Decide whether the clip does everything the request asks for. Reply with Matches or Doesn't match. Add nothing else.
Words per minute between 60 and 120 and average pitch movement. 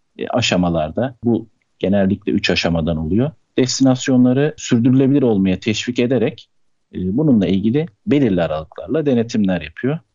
Doesn't match